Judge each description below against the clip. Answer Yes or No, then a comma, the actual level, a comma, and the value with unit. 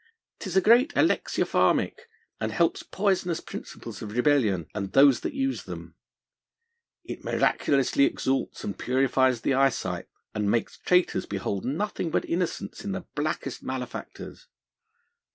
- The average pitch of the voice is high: No, low, 135 Hz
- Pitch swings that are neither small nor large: No, wide, 7.3 semitones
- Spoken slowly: Yes, slow, 130 wpm